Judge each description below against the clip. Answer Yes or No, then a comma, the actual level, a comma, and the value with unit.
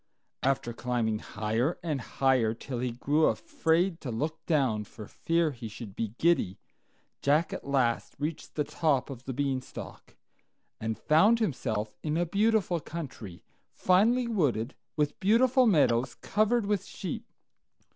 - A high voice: No, medium, 145 Hz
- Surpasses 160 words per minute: No, average, 140 wpm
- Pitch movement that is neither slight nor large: No, wide, 6.9 semitones